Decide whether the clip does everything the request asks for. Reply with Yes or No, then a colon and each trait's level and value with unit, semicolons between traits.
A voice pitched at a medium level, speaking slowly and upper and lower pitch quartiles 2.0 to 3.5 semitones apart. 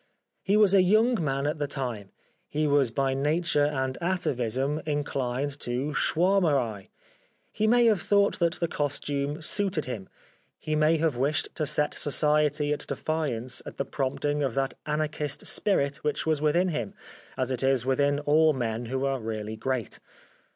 No: medium, 145 Hz; average, 165 wpm; average, 2.9 semitones